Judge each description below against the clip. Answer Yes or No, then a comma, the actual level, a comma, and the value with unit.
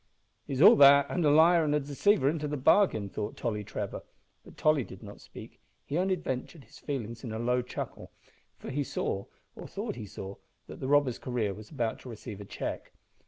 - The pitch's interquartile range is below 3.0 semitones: No, average, 5.3 semitones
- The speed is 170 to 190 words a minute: No, average, 200 wpm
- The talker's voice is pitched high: No, low, 130 Hz